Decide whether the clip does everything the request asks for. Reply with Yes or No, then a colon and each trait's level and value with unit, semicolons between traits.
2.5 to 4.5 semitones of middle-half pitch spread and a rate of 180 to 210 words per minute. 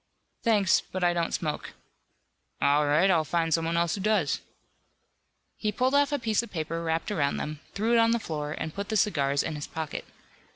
No: wide, 5.5 semitones; average, 200 wpm